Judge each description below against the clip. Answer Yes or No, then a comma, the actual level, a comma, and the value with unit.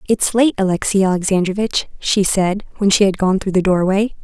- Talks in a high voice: Yes, high, 195 Hz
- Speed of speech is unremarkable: Yes, average, 185 wpm